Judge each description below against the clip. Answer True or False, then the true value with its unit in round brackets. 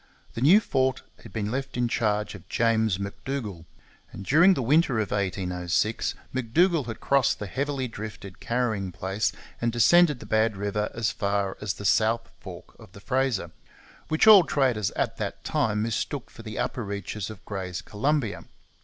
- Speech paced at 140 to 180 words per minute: True (170 wpm)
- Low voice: True (110 Hz)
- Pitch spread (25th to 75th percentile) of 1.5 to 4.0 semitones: False (4.6 semitones)